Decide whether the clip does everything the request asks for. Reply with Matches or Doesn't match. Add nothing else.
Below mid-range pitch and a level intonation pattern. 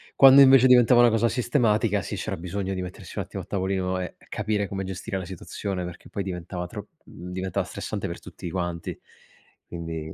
Doesn't match